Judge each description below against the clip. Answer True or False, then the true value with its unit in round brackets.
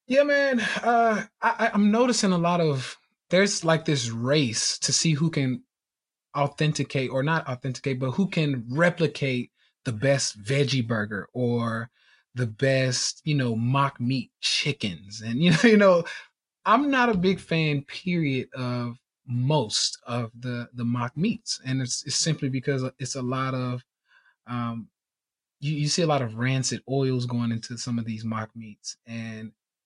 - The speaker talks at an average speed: True (165 wpm)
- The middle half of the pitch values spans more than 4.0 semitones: True (5.1 semitones)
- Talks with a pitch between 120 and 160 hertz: True (135 Hz)